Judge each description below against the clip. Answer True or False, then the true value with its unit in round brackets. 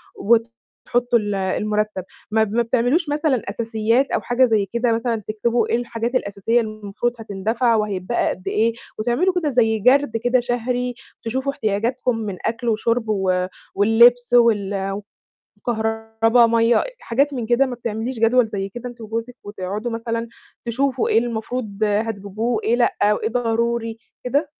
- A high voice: True (230 Hz)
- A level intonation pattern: True (2.2 semitones)